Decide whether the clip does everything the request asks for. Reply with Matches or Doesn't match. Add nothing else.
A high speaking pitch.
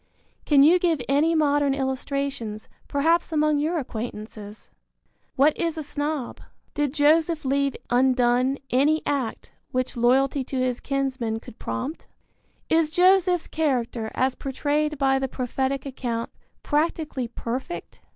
Matches